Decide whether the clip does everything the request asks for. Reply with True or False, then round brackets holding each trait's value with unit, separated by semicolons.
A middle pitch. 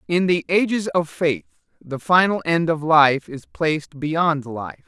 True (160 Hz)